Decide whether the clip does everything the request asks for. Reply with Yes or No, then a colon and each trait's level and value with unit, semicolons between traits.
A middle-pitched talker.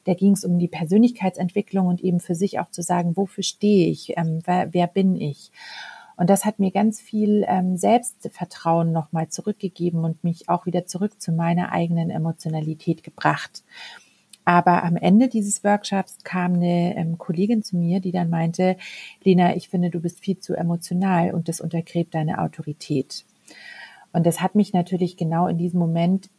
Yes: medium, 180 Hz